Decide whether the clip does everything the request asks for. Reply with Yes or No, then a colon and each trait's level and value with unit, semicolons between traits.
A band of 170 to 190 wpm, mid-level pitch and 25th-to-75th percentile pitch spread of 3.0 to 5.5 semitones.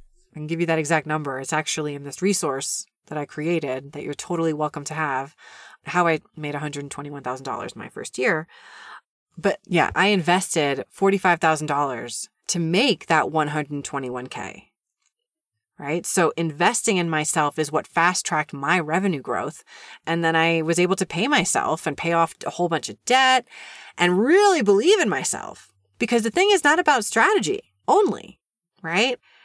Yes: average, 180 wpm; medium, 165 Hz; average, 4.7 semitones